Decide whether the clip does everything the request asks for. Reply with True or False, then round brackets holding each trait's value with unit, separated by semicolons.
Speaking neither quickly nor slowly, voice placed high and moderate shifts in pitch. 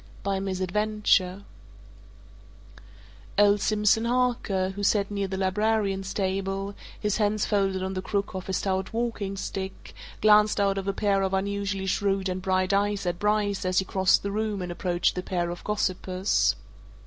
False (160 wpm; 195 Hz; 1.6 semitones)